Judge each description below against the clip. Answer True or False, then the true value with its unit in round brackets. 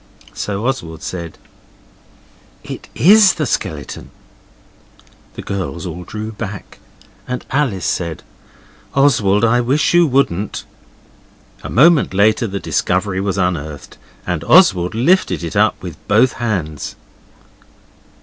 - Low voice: True (105 Hz)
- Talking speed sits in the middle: False (115 wpm)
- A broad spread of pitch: True (6.4 semitones)